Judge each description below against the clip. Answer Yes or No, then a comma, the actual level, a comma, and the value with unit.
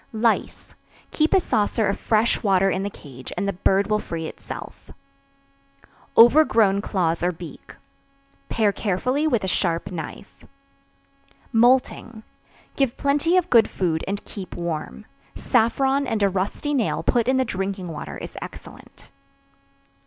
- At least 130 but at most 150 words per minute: Yes, average, 140 wpm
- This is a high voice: Yes, high, 205 Hz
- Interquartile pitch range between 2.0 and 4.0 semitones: No, average, 5.0 semitones